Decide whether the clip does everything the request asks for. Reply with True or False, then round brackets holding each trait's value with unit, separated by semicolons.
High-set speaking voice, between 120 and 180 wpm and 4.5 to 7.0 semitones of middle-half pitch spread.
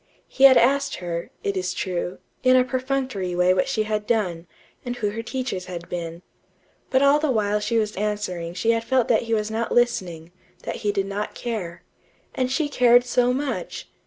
False (215 Hz; 195 wpm; 5.4 semitones)